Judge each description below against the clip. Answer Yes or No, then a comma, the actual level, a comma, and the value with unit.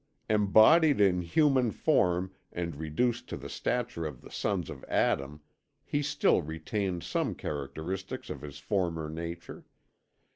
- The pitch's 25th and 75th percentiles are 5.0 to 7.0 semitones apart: Yes, wide, 5.5 semitones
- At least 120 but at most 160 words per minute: Yes, slow, 135 wpm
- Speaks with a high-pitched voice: No, very low, 90 Hz